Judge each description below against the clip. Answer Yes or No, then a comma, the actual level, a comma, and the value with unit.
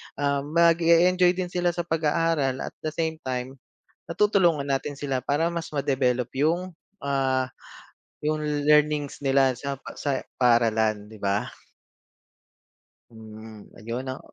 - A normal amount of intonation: Yes, average, 4.3 semitones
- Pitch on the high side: No, medium, 140 Hz